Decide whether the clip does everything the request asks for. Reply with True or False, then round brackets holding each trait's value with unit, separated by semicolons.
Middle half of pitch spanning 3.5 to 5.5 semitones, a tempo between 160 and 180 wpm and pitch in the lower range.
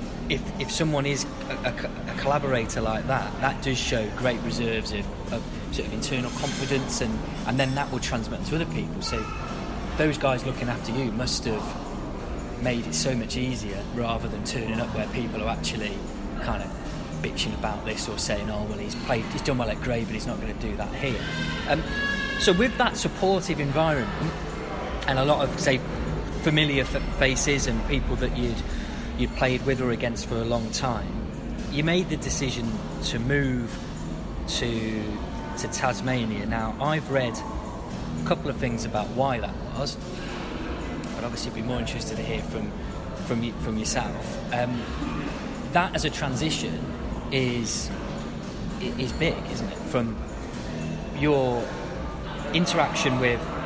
True (4.3 semitones; 165 wpm; 125 Hz)